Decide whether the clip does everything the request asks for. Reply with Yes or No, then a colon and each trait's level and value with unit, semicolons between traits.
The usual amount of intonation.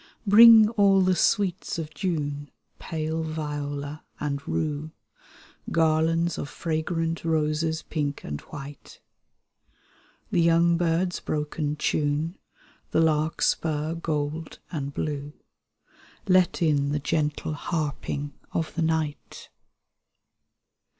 No: narrow, 2.1 semitones